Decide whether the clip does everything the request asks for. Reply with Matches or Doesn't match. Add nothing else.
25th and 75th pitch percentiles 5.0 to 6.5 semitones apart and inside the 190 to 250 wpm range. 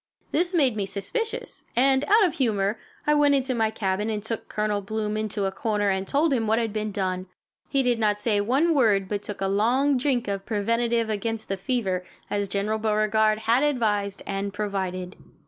Doesn't match